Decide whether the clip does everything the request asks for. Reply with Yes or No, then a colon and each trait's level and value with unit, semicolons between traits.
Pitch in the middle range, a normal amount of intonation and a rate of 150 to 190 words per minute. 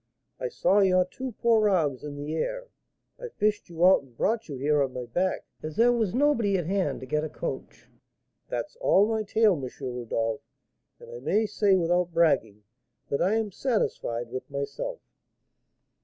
No: medium, 180 Hz; wide, 7.7 semitones; average, 180 wpm